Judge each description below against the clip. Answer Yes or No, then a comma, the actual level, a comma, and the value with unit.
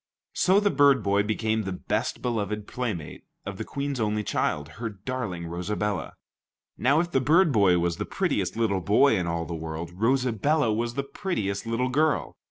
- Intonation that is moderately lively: No, wide, 5.9 semitones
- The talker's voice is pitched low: Yes, low, 110 Hz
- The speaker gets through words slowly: No, average, 175 wpm